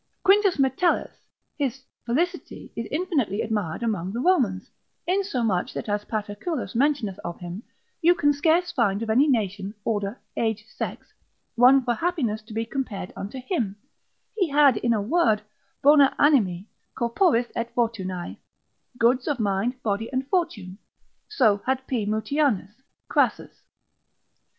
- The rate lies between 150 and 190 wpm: No, slow, 135 wpm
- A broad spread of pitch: Yes, wide, 5.7 semitones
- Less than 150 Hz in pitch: No, high, 235 Hz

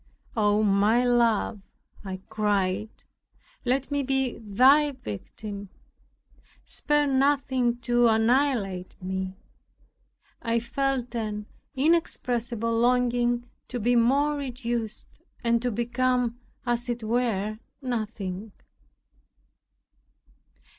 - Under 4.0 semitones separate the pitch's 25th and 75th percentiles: Yes, average, 2.9 semitones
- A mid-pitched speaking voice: No, high, 240 Hz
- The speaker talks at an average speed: No, slow, 90 wpm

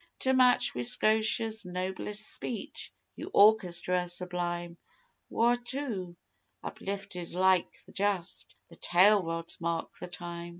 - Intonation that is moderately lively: Yes, average, 3.9 semitones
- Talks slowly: Yes, slow, 115 wpm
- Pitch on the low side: No, medium, 185 Hz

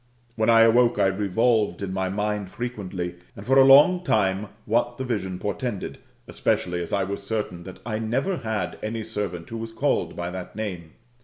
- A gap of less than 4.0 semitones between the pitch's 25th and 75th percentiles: Yes, average, 3.6 semitones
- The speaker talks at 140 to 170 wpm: No, average, 185 wpm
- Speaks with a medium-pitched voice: No, low, 105 Hz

